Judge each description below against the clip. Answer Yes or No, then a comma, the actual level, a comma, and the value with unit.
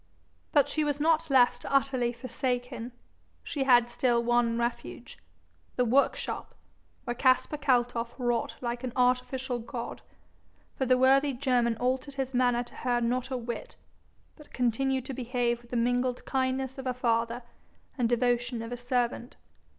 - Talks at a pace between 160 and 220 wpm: No, average, 150 wpm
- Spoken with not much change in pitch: Yes, narrow, 1.6 semitones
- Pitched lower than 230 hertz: No, very high, 250 Hz